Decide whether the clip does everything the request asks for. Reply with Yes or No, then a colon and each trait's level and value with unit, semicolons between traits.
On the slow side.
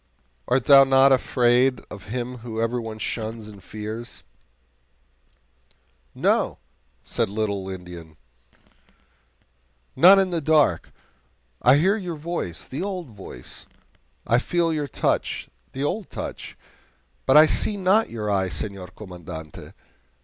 Yes: slow, 125 wpm